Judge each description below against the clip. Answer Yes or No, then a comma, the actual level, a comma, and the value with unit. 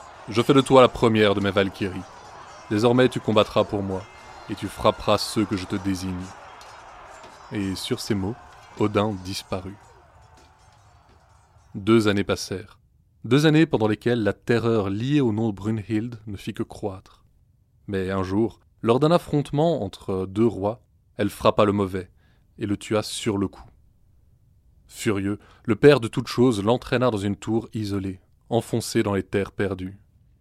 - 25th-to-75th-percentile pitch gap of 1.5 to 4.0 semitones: Yes, average, 3.1 semitones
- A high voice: No, low, 105 Hz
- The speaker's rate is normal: Yes, average, 160 wpm